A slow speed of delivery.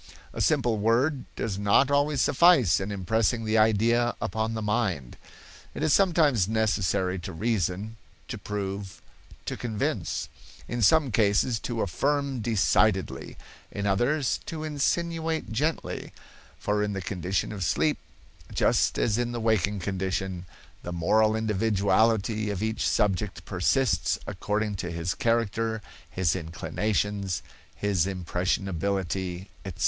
Yes: slow, 125 wpm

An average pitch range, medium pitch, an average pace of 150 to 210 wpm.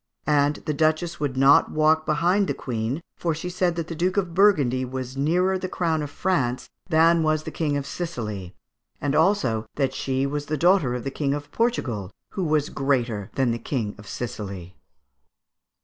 Yes: average, 4.7 semitones; medium, 145 Hz; average, 180 wpm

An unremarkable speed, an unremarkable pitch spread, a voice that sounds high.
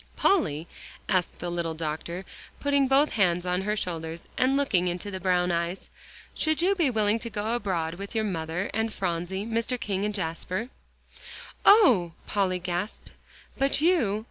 Yes: average, 160 wpm; average, 4.8 semitones; high, 195 Hz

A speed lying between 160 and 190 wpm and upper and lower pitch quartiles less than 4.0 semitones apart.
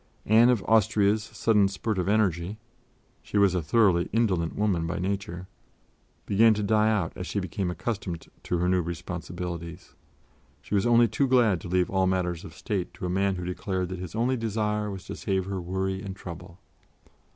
Yes: average, 185 wpm; average, 3.0 semitones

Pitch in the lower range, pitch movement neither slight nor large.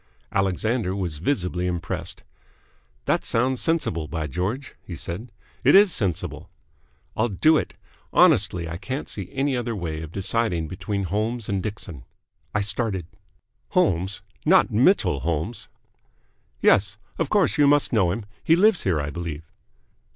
No: low, 100 Hz; wide, 6.1 semitones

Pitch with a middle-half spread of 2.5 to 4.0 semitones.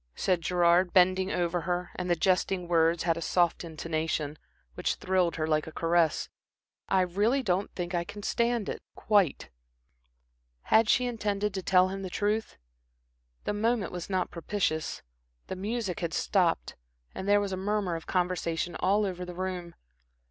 Yes: average, 2.8 semitones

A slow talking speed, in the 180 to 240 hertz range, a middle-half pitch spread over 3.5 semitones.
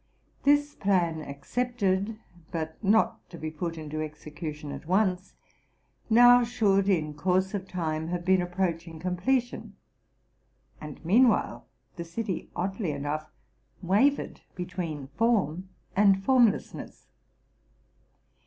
Yes: slow, 115 wpm; medium, 185 Hz; average, 4.7 semitones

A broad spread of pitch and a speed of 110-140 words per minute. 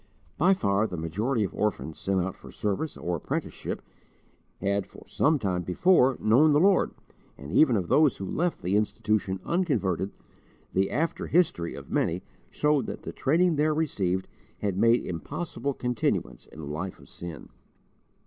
No: wide, 8.2 semitones; average, 160 wpm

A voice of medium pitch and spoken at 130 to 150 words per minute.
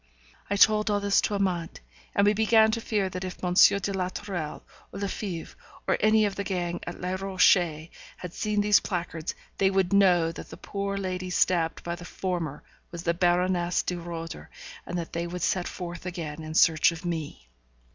No: medium, 180 Hz; average, 195 wpm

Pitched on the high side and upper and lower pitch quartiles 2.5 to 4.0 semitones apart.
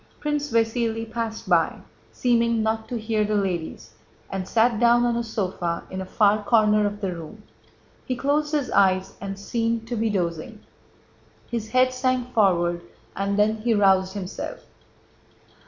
Yes: high, 220 Hz; average, 3.3 semitones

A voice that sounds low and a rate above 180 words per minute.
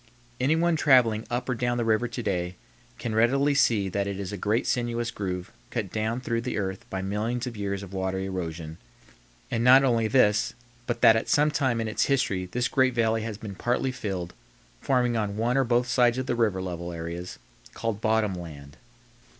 Yes: low, 110 Hz; average, 200 wpm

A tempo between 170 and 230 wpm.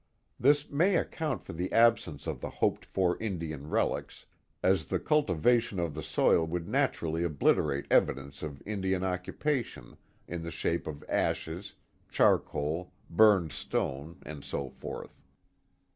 No: average, 140 wpm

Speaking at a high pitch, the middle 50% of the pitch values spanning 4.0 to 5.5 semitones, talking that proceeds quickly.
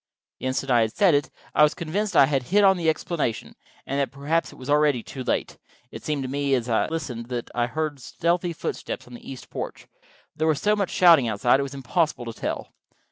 No: medium, 140 Hz; average, 4.4 semitones; fast, 240 wpm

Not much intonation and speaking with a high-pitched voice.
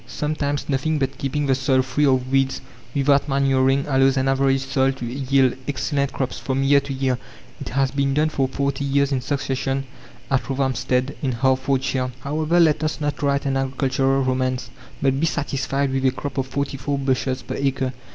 No: narrow, 1.1 semitones; low, 135 Hz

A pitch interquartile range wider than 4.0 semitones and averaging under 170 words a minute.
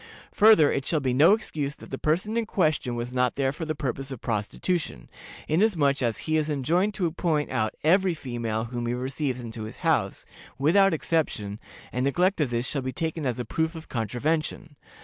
No: average, 4.9 semitones; average, 195 wpm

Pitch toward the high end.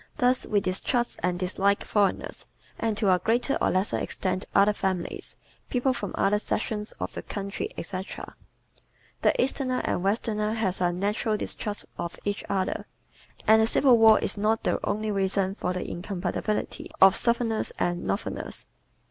Yes: high, 205 Hz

